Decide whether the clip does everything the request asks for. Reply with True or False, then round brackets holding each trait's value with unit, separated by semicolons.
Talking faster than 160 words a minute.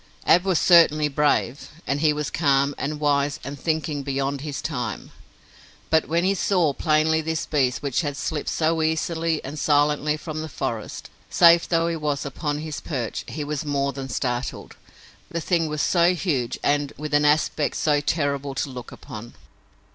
True (175 wpm)